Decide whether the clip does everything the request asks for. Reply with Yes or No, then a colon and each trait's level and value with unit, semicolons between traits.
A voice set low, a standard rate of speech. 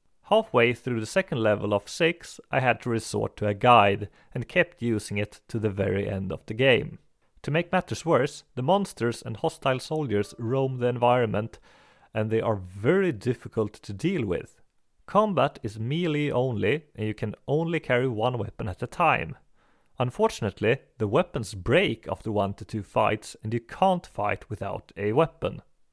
Yes: low, 120 Hz; average, 175 wpm